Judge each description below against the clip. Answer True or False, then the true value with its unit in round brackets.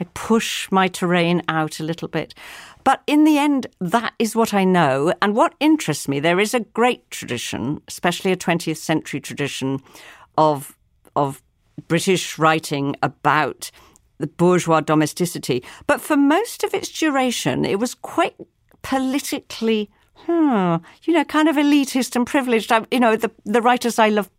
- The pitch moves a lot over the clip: True (8.8 semitones)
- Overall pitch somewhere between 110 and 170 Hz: False (210 Hz)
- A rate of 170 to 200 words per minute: False (160 wpm)